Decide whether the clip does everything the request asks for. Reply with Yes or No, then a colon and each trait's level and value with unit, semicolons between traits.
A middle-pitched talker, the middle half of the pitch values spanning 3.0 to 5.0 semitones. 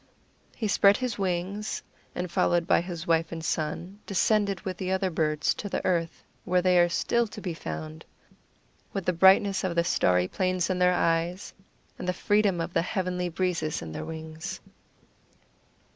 No: medium, 180 Hz; narrow, 2.4 semitones